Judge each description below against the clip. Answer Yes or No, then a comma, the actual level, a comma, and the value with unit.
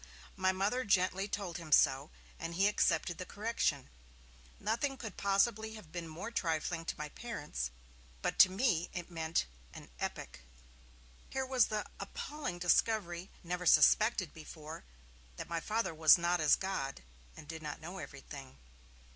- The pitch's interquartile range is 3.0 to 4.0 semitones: No, average, 4.8 semitones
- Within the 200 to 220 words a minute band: No, average, 150 wpm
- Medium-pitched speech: Yes, medium, 180 Hz